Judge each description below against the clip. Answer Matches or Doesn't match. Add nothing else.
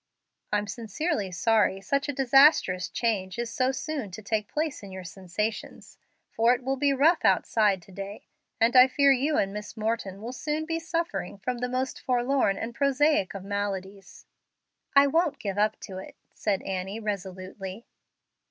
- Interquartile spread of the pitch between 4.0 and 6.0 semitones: Matches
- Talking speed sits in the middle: Matches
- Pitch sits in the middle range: Doesn't match